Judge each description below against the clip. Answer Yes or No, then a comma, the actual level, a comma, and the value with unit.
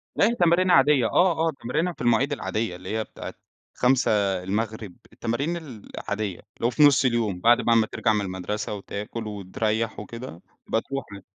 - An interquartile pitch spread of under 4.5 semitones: No, average, 4.8 semitones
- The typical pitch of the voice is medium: No, low, 115 Hz